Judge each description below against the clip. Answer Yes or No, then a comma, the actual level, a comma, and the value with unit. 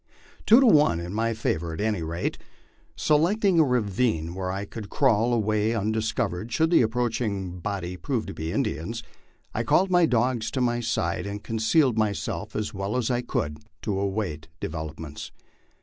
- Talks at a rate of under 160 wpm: No, average, 170 wpm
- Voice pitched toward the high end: No, low, 110 Hz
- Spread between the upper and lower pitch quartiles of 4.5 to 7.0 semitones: Yes, average, 4.8 semitones